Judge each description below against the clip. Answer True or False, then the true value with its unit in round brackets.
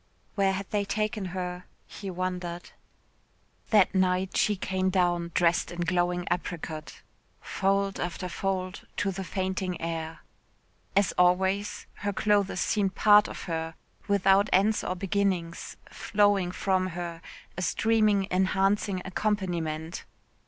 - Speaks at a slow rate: True (125 wpm)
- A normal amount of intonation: False (2.1 semitones)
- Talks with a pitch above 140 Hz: True (185 Hz)